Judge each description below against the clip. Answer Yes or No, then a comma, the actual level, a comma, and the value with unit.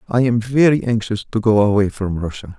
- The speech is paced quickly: Yes, fast, 210 wpm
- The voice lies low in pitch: Yes, low, 110 Hz